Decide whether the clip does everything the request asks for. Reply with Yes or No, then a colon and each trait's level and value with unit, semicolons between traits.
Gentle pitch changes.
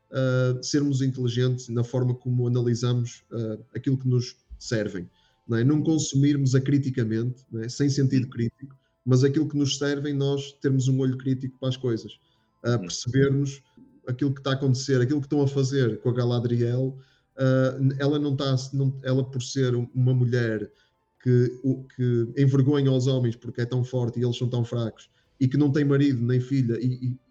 Yes: narrow, 2.1 semitones